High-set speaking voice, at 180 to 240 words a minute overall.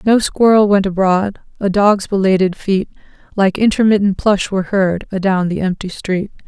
No: high, 195 Hz; average, 155 wpm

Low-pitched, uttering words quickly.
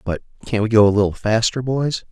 Yes: low, 110 Hz; fast, 225 wpm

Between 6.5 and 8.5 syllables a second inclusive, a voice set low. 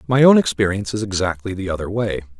Yes: 6.8 syllables/s; low, 100 Hz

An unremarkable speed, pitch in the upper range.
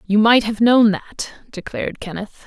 Yes: average, 170 wpm; high, 215 Hz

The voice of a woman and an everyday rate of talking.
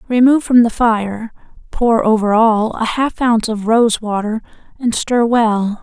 Yes: female; average, 165 wpm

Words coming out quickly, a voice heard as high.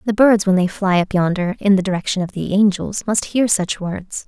Yes: fast, 240 wpm; high, 195 Hz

